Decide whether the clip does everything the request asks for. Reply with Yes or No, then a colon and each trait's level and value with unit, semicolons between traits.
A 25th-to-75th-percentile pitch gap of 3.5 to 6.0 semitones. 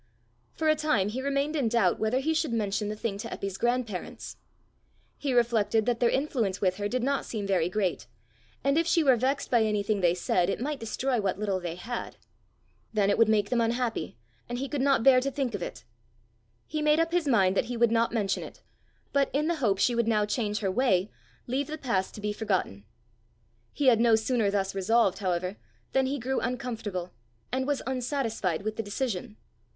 Yes: average, 4.6 semitones